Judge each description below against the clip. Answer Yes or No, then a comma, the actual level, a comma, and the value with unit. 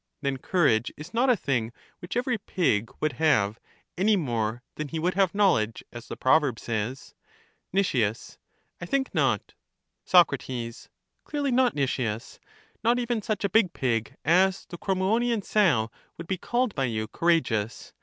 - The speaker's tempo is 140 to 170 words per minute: Yes, average, 155 wpm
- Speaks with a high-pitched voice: No, medium, 160 Hz